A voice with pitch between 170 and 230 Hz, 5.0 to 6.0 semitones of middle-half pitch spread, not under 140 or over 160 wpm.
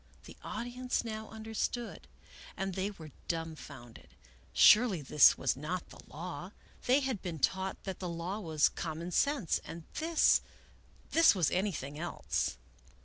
Yes: medium, 185 Hz; average, 5.3 semitones; average, 145 wpm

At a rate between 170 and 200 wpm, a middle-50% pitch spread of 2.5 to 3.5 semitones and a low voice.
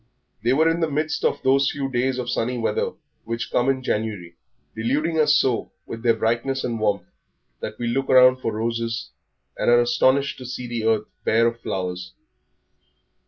Yes: average, 180 wpm; average, 2.8 semitones; low, 120 Hz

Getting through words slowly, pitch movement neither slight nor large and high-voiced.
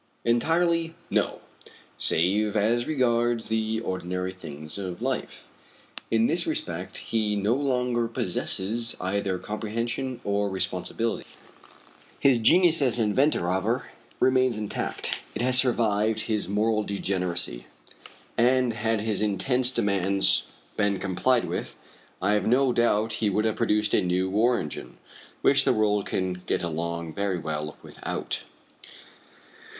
No: slow, 130 wpm; average, 3.9 semitones; low, 110 Hz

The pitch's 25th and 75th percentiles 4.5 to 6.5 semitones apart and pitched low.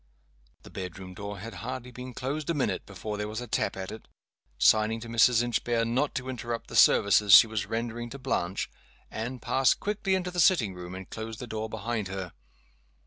No: average, 3.6 semitones; low, 115 Hz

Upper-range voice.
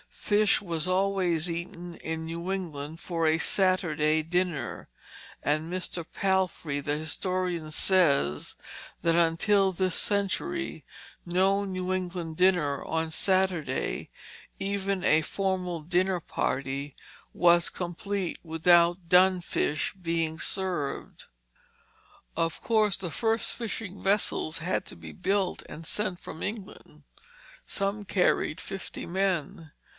No: medium, 175 Hz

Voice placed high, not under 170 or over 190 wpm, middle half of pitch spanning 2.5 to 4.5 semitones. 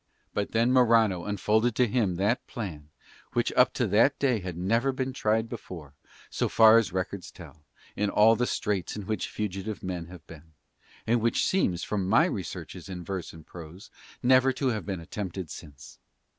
No: low, 100 Hz; average, 180 wpm; average, 4.2 semitones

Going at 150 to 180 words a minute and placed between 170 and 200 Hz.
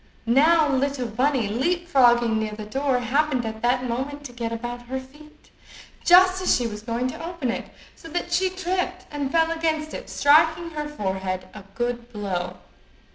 No: average, 175 wpm; very high, 265 Hz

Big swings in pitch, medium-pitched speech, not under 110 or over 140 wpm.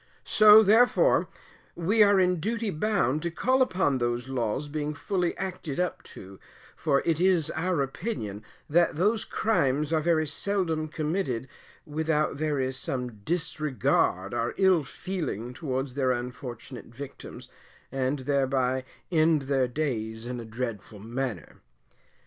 Yes: wide, 5.7 semitones; medium, 150 Hz; slow, 135 wpm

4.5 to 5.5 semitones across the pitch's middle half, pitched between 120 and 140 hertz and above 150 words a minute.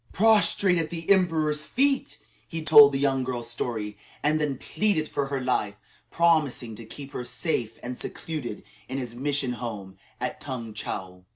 Yes: average, 4.9 semitones; low, 135 Hz; average, 165 wpm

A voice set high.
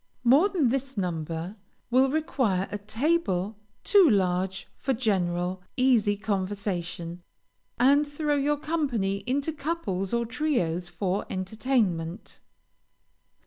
Yes: high, 215 Hz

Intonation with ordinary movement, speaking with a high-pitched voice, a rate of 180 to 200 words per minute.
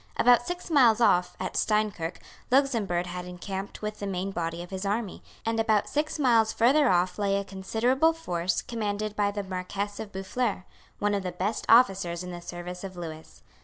Yes: average, 3.9 semitones; high, 200 Hz; average, 185 wpm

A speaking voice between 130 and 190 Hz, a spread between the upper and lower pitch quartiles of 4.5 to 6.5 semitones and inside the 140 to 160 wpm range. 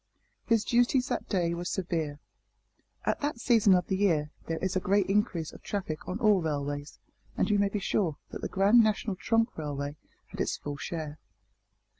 No: medium, 185 Hz; average, 4.9 semitones; average, 185 wpm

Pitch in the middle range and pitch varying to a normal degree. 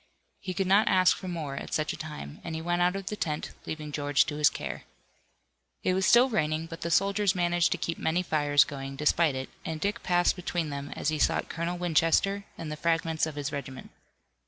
Yes: medium, 165 Hz; average, 3.2 semitones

